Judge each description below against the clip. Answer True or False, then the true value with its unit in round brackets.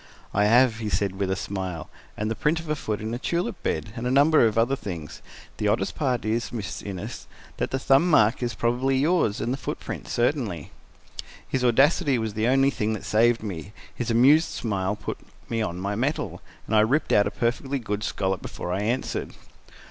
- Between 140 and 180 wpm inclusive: False (205 wpm)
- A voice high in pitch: False (115 Hz)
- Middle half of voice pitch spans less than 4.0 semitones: False (4.3 semitones)